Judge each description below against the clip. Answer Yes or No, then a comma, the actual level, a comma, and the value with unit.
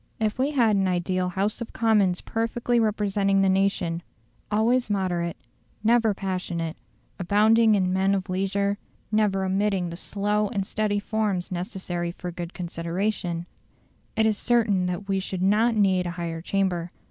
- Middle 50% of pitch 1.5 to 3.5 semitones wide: Yes, average, 2.8 semitones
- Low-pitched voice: No, high, 195 Hz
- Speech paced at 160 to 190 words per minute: No, average, 150 wpm